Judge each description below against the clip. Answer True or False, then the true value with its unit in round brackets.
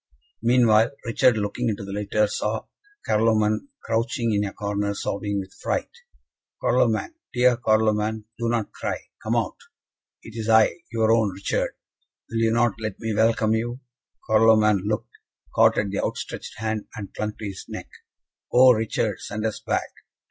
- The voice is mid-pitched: False (110 Hz)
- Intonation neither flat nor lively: False (1.6 semitones)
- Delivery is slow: False (155 wpm)